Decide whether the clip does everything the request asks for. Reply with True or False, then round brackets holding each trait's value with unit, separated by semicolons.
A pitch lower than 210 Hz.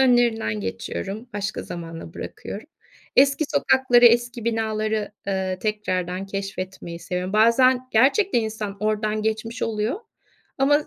False (215 Hz)